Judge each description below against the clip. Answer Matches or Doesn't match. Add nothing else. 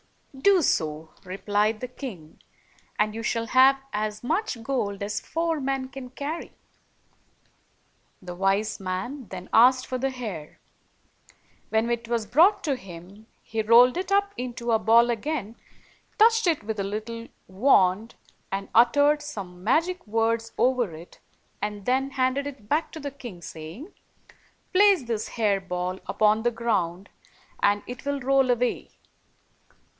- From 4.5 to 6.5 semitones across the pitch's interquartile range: Matches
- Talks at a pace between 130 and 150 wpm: Matches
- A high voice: Matches